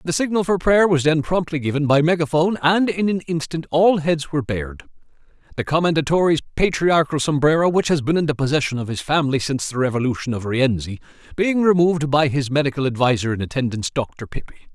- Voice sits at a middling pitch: Yes, medium, 150 Hz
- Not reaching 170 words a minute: No, average, 185 wpm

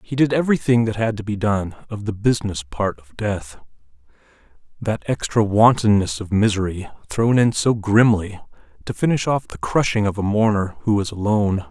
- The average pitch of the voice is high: No, low, 105 Hz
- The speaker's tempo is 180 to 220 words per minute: No, average, 170 wpm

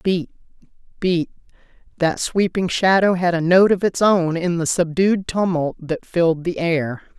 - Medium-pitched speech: Yes, medium, 175 Hz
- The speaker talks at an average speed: Yes, average, 160 wpm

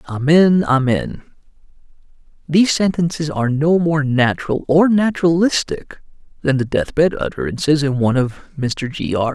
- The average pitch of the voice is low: No, medium, 150 Hz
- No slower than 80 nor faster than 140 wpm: Yes, slow, 135 wpm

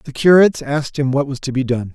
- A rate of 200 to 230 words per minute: No, fast, 275 wpm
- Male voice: Yes, male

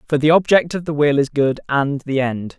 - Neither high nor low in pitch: Yes, medium, 145 Hz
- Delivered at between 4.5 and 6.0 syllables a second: Yes, 5.2 syllables/s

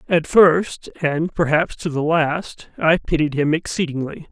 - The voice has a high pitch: No, medium, 160 Hz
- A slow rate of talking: No, average, 155 wpm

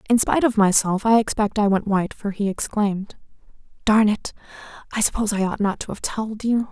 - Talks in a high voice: Yes, high, 210 Hz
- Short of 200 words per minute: No, fast, 205 wpm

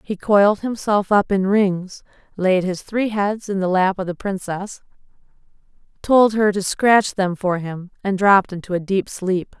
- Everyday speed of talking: Yes, average, 180 wpm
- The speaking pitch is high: Yes, high, 195 Hz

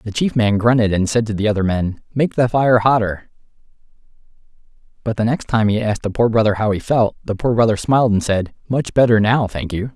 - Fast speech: Yes, fast, 225 wpm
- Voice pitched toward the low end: Yes, low, 110 Hz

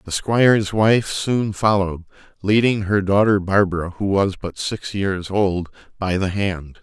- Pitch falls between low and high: No, low, 100 Hz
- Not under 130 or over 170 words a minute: Yes, average, 160 wpm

